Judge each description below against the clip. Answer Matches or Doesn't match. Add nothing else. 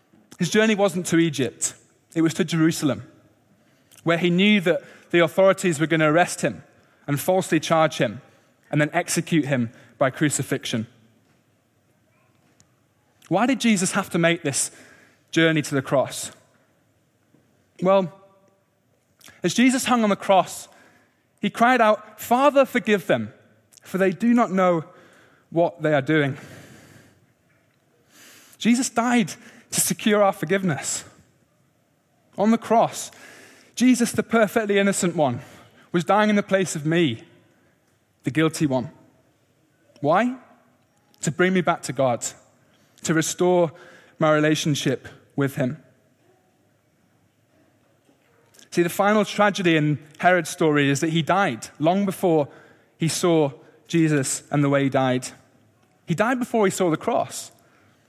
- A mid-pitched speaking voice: Matches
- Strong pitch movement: Matches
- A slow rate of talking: Matches